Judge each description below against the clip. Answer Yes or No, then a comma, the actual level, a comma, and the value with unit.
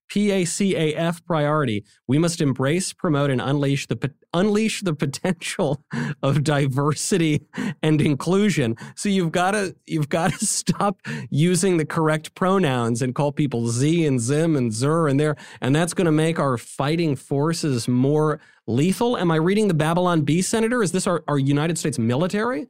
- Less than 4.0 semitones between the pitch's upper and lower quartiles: No, average, 4.3 semitones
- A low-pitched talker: No, medium, 155 Hz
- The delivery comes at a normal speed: Yes, average, 165 wpm